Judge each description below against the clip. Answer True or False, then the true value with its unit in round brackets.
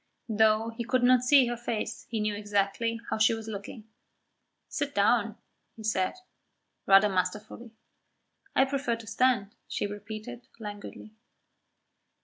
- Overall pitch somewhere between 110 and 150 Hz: False (220 Hz)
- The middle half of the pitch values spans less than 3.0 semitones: True (2.5 semitones)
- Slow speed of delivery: True (130 wpm)